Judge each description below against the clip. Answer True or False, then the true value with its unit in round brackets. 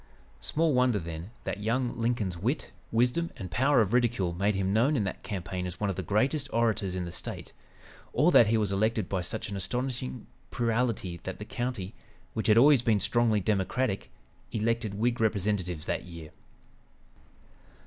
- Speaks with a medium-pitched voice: False (110 Hz)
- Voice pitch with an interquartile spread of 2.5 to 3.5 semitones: False (4.2 semitones)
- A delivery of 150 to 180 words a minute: True (170 wpm)